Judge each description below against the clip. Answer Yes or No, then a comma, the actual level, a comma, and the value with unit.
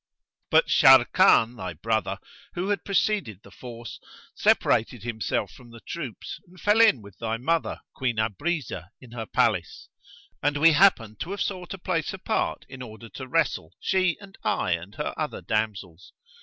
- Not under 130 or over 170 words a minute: Yes, average, 165 wpm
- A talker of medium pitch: No, low, 125 Hz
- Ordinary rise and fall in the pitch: No, wide, 7.9 semitones